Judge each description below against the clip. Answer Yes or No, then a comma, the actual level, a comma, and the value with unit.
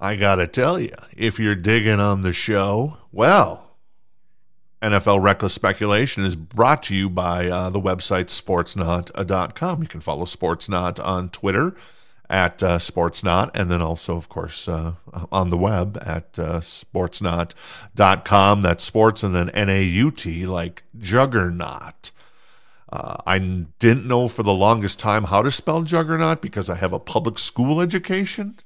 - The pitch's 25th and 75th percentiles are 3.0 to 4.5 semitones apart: Yes, average, 4.2 semitones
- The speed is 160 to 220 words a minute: No, average, 145 wpm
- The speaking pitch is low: Yes, low, 100 Hz